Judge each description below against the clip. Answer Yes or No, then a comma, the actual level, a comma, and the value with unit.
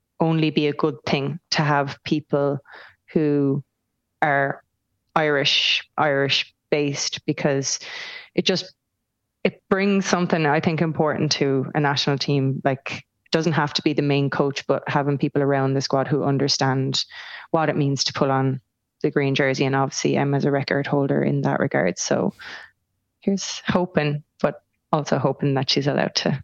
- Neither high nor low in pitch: Yes, medium, 145 Hz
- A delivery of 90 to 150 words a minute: No, average, 165 wpm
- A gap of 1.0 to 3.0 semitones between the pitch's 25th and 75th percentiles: Yes, narrow, 2.6 semitones